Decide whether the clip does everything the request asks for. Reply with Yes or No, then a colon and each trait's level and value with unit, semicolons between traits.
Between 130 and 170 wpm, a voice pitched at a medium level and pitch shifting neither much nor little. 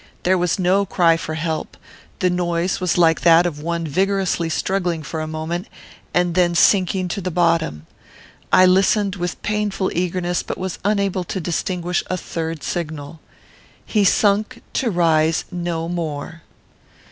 No: average, 150 wpm; medium, 175 Hz; narrow, 2.3 semitones